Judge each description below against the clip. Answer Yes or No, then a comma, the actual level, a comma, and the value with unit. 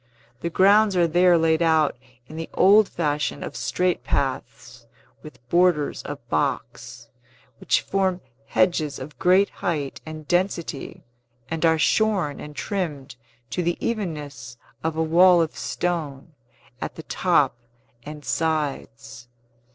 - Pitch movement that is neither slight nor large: Yes, average, 3.7 semitones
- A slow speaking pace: Yes, slow, 130 wpm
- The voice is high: No, medium, 160 Hz